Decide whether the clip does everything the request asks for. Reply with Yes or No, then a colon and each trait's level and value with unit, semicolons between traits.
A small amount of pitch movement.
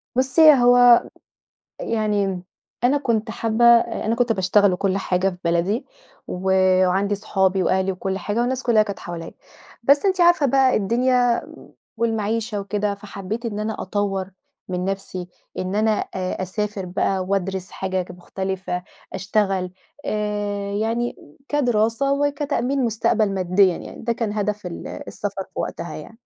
No: average, 3.6 semitones